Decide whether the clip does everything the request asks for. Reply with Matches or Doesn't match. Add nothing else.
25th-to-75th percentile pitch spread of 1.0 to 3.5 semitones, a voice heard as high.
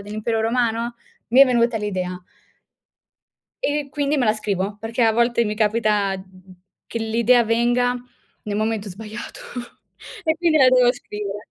Matches